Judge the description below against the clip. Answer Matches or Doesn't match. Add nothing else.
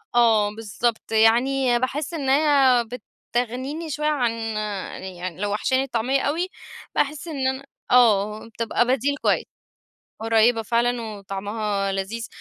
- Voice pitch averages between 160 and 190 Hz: Doesn't match